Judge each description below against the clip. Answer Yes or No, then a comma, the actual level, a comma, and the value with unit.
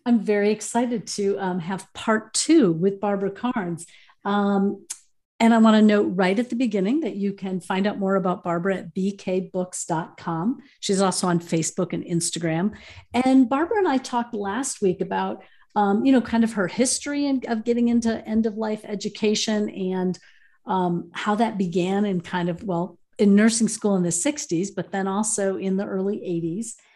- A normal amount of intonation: Yes, average, 3.5 semitones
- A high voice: Yes, high, 200 Hz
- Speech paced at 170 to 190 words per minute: Yes, average, 185 wpm